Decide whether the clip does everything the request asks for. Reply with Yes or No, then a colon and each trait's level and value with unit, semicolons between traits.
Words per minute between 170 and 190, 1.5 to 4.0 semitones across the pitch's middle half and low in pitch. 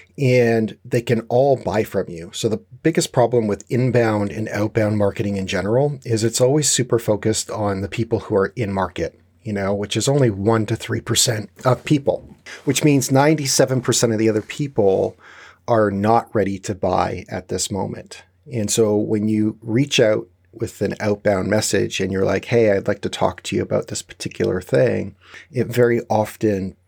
Yes: average, 185 wpm; average, 3.1 semitones; low, 110 Hz